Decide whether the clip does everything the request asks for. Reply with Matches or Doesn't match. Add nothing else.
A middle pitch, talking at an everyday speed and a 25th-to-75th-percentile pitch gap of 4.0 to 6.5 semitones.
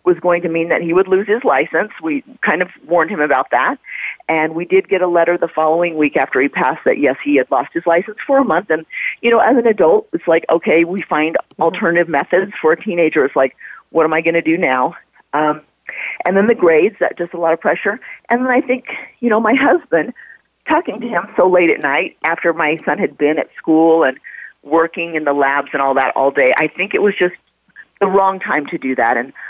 Doesn't match